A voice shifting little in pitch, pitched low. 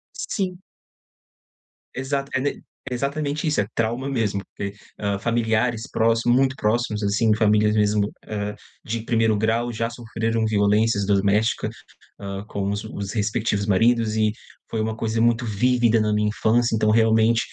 Yes: narrow, 2.1 semitones; low, 110 Hz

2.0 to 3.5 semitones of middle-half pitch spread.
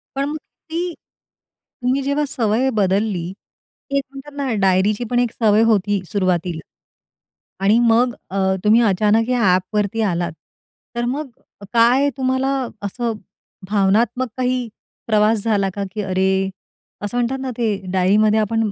No: average, 4.0 semitones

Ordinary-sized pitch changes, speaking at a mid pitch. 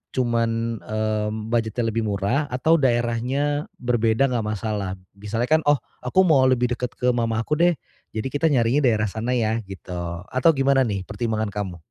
No: average, 3.1 semitones; low, 115 Hz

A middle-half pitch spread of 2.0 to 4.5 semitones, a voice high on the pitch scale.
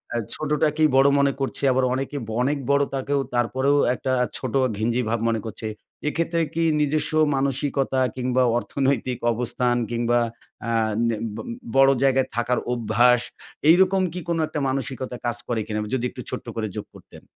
No: average, 2.8 semitones; low, 130 Hz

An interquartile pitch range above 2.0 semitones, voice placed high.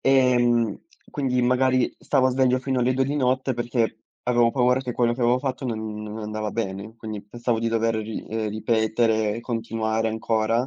No: narrow, 2.5 semitones; low, 115 Hz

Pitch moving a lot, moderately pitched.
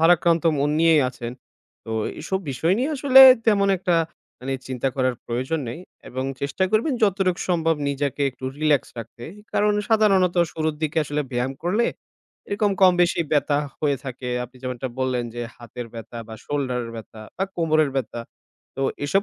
Yes: wide, 6.0 semitones; medium, 150 Hz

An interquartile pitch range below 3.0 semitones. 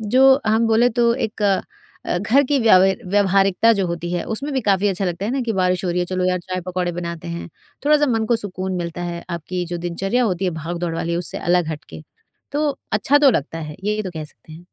No: average, 4.4 semitones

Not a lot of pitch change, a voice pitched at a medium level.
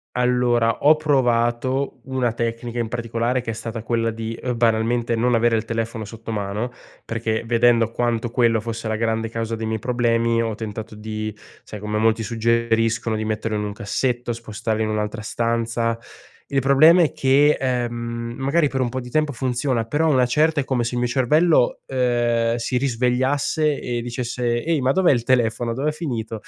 No: narrow, 1.9 semitones; low, 120 Hz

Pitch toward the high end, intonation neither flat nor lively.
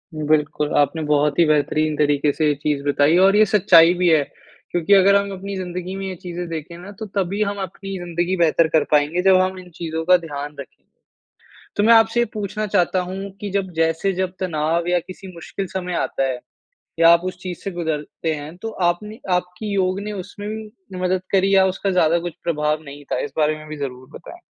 No: medium, 175 Hz; average, 3.8 semitones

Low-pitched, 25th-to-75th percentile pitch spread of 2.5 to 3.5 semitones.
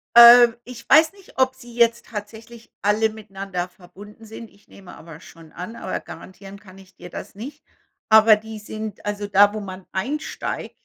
No: high, 215 Hz; average, 3.2 semitones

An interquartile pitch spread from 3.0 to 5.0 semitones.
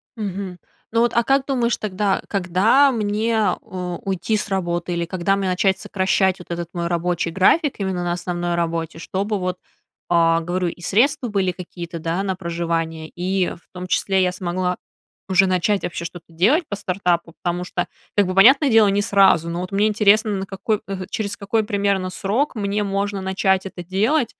No: narrow, 2.6 semitones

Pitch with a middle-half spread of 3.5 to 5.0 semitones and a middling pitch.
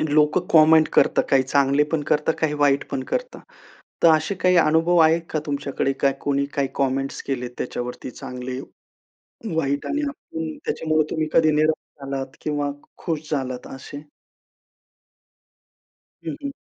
No: average, 2.7 semitones; medium, 150 Hz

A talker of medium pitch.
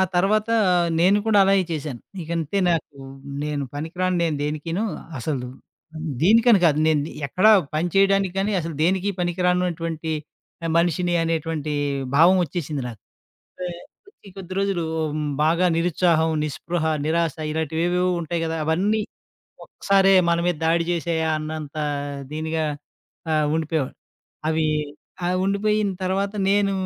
Yes: medium, 170 Hz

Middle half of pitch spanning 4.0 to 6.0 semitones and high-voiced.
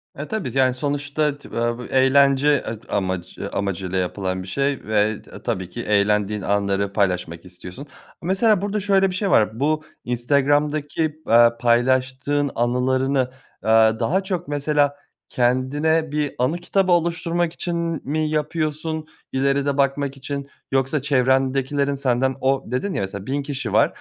No: average, 4.3 semitones; low, 135 Hz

